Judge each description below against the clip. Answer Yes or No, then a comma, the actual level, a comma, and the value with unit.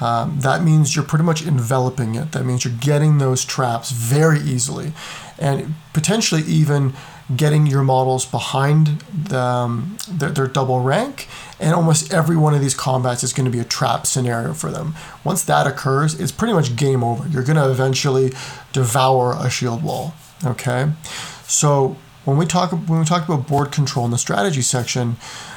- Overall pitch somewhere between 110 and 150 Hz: Yes, medium, 140 Hz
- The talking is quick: No, average, 180 wpm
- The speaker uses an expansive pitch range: No, average, 3.5 semitones